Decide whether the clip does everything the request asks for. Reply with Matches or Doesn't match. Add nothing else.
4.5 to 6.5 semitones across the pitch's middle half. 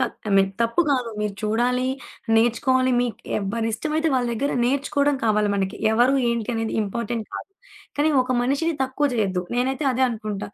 Doesn't match